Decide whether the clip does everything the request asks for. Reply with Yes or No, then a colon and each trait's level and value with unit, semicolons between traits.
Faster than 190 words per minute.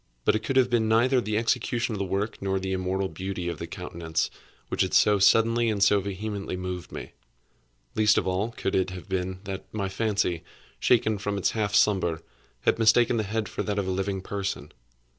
Yes: fast, 205 wpm